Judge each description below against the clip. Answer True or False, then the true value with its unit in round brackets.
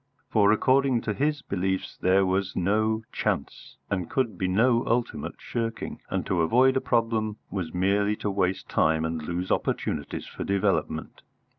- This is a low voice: True (100 Hz)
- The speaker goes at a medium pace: True (155 wpm)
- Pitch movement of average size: True (3.8 semitones)